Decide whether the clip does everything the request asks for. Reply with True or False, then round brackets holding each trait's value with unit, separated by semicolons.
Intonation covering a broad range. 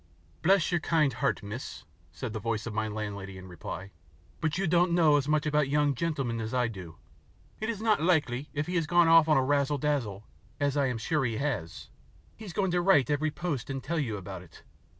True (6.5 semitones)